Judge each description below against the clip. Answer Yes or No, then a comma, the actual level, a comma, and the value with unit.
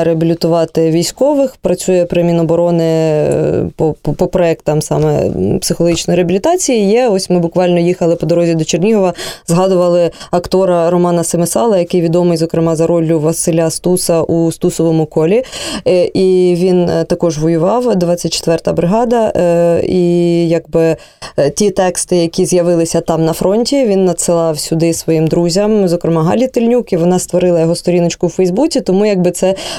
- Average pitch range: No, narrow, 1.9 semitones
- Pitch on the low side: No, medium, 175 Hz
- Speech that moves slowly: No, average, 135 wpm